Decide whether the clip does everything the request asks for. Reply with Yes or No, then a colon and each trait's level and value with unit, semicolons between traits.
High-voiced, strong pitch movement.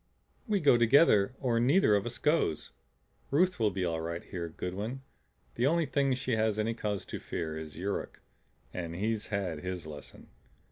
No: low, 105 Hz; wide, 6.4 semitones